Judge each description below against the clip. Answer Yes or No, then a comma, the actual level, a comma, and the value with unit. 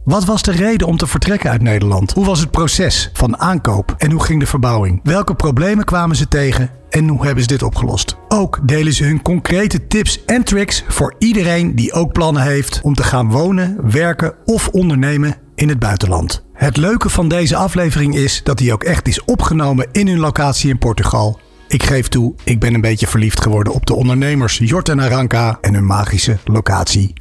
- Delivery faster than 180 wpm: Yes, fast, 200 wpm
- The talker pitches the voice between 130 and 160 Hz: Yes, medium, 140 Hz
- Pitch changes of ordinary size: No, wide, 6.6 semitones